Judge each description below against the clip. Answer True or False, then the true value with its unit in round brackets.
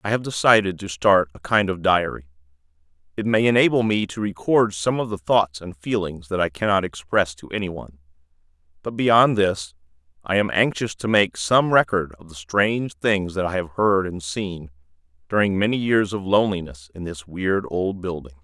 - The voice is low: True (95 Hz)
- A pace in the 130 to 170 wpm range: False (185 wpm)